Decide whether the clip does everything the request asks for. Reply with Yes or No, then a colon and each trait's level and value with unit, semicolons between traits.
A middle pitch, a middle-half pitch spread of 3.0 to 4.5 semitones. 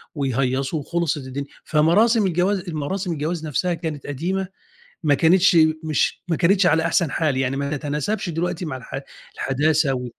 Yes: medium, 155 Hz; average, 3.9 semitones